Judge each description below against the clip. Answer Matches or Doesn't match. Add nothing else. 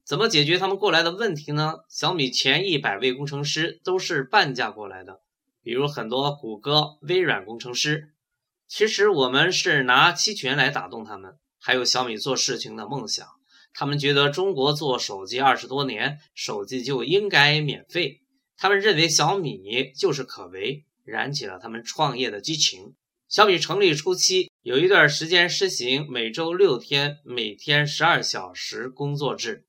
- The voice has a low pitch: Doesn't match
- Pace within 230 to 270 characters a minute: Matches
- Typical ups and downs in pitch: Doesn't match